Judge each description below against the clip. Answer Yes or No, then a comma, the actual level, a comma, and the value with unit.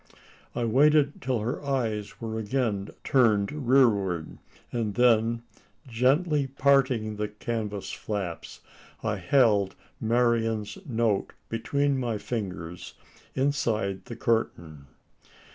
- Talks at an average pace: No, slow, 100 wpm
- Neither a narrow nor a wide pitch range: Yes, average, 3.8 semitones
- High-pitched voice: No, low, 115 Hz